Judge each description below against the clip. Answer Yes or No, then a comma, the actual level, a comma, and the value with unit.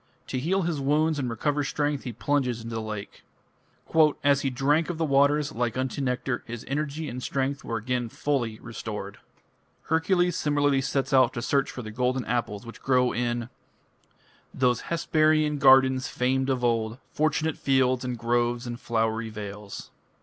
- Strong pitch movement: No, average, 3.4 semitones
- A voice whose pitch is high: No, low, 130 Hz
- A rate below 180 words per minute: Yes, average, 165 wpm